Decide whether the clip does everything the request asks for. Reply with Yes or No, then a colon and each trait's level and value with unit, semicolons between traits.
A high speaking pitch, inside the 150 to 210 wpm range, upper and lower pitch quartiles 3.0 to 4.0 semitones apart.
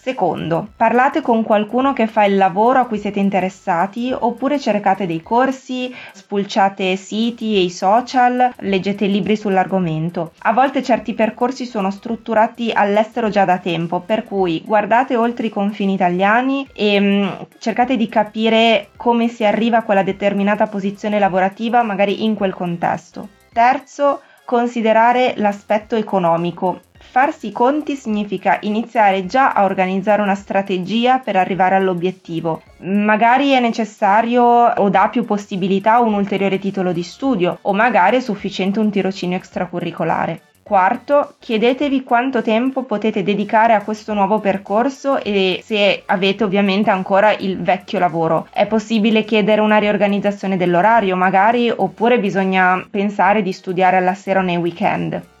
No: high, 210 Hz; average, 140 wpm; average, 3.3 semitones